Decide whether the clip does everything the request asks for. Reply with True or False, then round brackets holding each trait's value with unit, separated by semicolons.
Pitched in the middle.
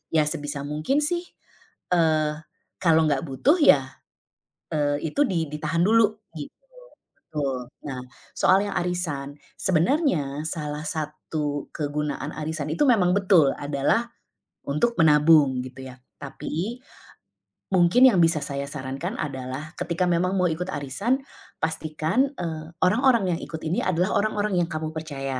True (155 Hz)